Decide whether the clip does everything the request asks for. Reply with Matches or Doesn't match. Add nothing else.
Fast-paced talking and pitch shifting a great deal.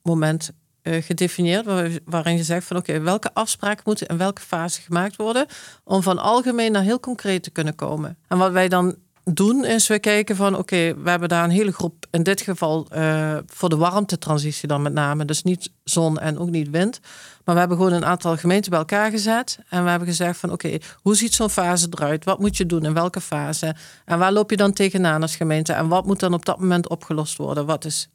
Doesn't match